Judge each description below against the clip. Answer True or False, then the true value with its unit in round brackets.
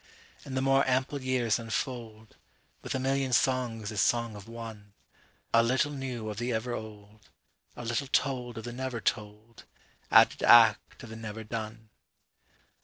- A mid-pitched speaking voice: False (115 Hz)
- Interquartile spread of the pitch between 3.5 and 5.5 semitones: False (2.9 semitones)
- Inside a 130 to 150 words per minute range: True (140 wpm)